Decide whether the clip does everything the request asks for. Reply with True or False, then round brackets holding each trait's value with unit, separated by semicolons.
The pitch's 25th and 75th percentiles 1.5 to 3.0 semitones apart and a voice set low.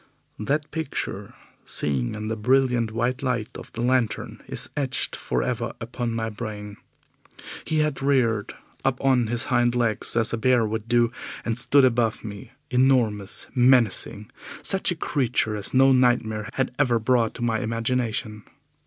True (2.7 semitones; 120 Hz)